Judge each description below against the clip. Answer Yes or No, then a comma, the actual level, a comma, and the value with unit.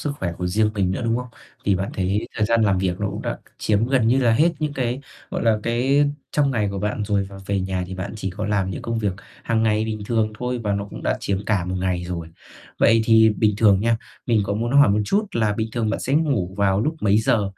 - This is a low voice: Yes, low, 105 Hz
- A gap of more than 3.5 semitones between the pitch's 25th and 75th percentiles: No, average, 3.1 semitones